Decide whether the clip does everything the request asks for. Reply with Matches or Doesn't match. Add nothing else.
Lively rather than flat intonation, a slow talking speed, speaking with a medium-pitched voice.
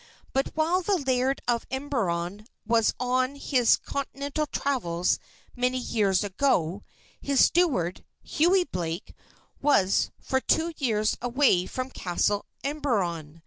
Doesn't match